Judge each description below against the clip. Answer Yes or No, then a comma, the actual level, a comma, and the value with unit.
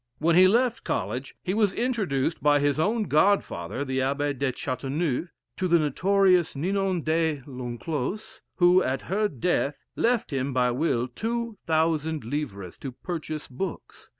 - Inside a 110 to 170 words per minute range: Yes, average, 150 wpm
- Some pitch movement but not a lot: No, wide, 5.8 semitones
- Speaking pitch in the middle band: Yes, medium, 155 Hz